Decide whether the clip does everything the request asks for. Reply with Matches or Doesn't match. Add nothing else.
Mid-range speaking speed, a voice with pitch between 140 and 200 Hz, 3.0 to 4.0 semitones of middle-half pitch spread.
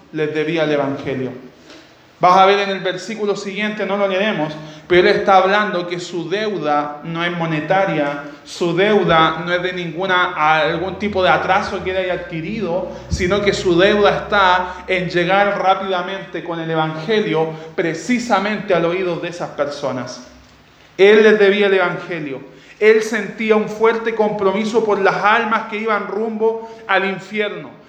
Matches